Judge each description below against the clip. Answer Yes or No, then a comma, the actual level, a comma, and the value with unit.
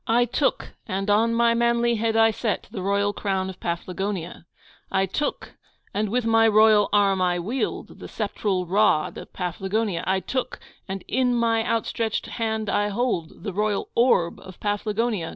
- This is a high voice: Yes, high, 210 Hz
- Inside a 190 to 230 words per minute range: No, average, 165 wpm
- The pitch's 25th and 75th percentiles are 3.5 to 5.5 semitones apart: No, average, 3.0 semitones